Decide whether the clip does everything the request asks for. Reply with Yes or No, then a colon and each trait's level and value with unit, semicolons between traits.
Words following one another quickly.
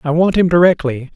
Yes: fast, 210 wpm